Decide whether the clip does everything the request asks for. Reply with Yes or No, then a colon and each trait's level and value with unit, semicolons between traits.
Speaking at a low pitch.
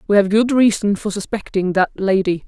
No: high, 200 Hz